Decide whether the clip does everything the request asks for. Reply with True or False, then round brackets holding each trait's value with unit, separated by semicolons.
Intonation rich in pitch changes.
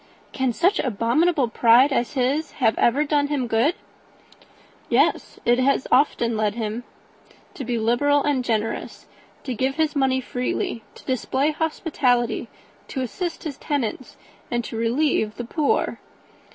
False (3.6 semitones)